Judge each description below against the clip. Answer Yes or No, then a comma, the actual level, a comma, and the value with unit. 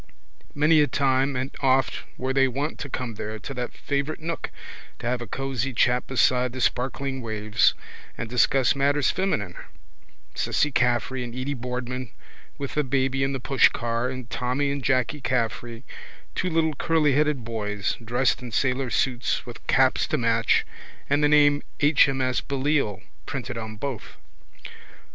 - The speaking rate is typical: Yes, average, 155 wpm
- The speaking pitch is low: Yes, low, 130 Hz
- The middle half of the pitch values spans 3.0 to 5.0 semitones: No, narrow, 2.6 semitones